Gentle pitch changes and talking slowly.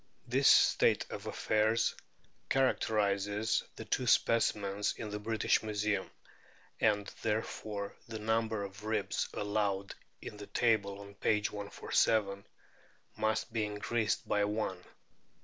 Yes: narrow, 1.5 semitones; slow, 115 wpm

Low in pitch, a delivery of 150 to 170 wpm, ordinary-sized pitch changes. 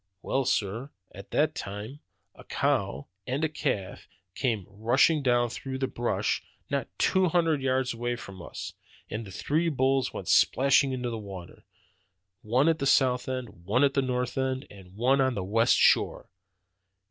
Yes: low, 125 Hz; average, 165 wpm; average, 3.9 semitones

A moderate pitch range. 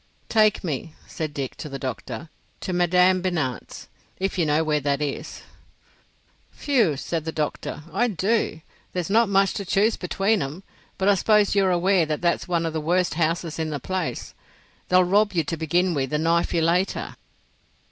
Yes: average, 3.7 semitones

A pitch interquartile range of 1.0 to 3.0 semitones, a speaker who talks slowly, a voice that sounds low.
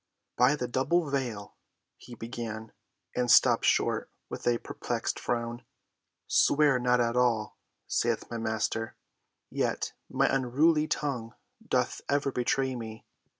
Yes: average, 2.7 semitones; slow, 125 wpm; low, 125 Hz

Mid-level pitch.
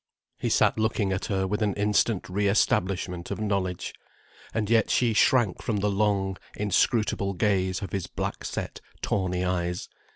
No: low, 100 Hz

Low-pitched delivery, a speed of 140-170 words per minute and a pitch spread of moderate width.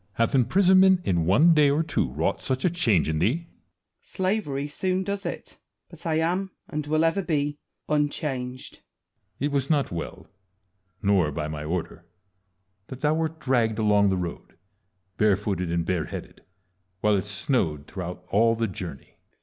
No: low, 125 Hz; average, 160 wpm; wide, 9.0 semitones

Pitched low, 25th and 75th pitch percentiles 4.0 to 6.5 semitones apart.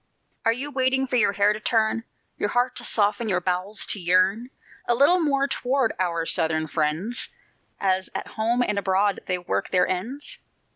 No: high, 210 Hz; average, 5.1 semitones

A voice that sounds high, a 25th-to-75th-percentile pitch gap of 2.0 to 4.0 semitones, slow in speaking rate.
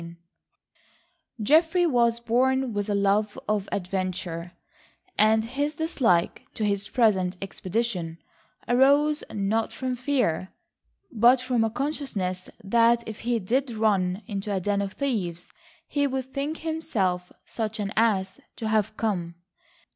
No: high, 220 Hz; average, 4.8 semitones; slow, 130 wpm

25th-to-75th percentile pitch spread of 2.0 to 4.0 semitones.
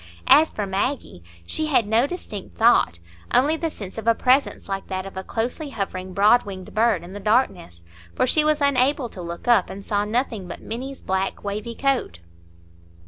No: wide, 5.4 semitones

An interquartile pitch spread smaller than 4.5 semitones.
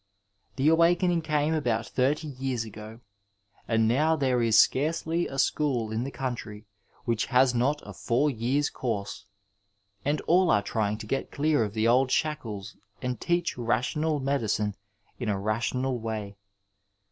No: average, 4.9 semitones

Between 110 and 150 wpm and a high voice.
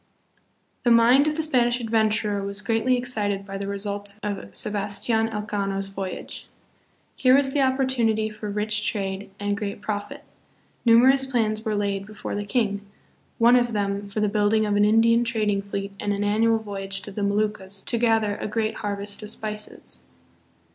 No: average, 170 wpm; high, 210 Hz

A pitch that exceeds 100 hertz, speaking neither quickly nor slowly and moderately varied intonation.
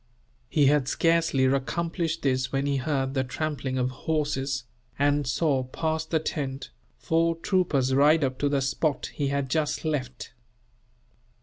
Yes: medium, 140 Hz; average, 145 wpm; average, 3.0 semitones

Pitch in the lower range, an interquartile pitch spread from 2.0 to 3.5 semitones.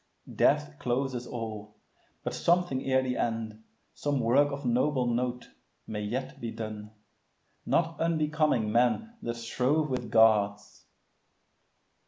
No: low, 125 Hz; average, 3.9 semitones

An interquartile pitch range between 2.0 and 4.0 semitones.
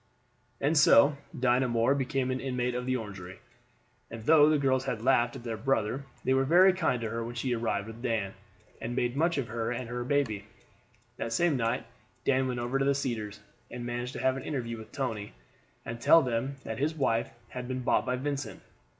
Yes: average, 2.8 semitones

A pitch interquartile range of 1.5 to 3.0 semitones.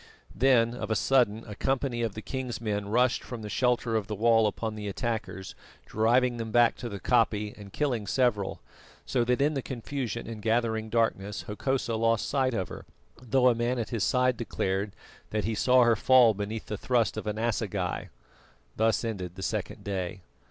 Yes: average, 2.7 semitones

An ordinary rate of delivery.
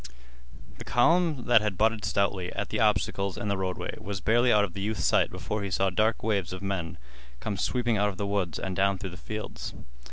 No: fast, 220 wpm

